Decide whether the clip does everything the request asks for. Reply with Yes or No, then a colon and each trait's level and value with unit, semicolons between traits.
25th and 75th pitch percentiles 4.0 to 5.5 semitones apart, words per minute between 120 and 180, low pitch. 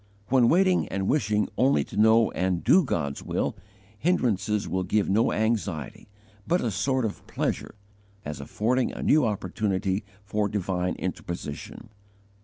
Yes: average, 4.4 semitones; average, 140 wpm; low, 105 Hz